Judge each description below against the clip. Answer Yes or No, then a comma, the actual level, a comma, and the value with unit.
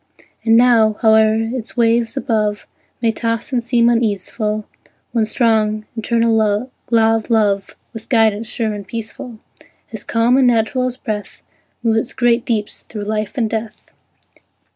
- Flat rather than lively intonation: Yes, narrow, 1.6 semitones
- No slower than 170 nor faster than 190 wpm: No, average, 145 wpm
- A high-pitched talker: Yes, high, 225 Hz